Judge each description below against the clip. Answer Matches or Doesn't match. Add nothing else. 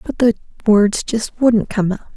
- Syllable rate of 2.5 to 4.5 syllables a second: Matches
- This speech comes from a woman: Matches